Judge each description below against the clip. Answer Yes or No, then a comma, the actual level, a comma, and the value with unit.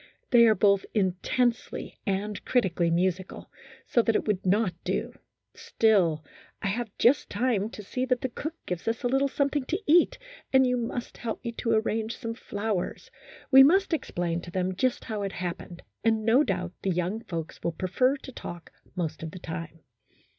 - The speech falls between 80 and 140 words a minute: No, average, 185 wpm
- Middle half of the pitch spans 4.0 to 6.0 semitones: Yes, average, 5.3 semitones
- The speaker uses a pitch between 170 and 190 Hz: No, high, 215 Hz